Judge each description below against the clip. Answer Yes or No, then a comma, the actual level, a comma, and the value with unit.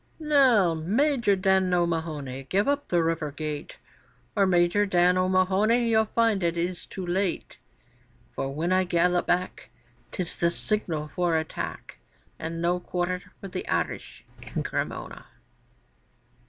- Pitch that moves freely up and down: No, average, 2.9 semitones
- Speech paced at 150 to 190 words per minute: No, slow, 135 wpm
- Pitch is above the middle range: No, medium, 180 Hz